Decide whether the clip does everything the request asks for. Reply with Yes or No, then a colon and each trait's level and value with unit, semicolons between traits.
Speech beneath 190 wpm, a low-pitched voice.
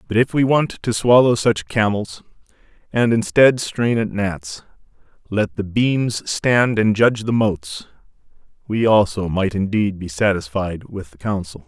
Yes: average, 155 wpm; low, 105 Hz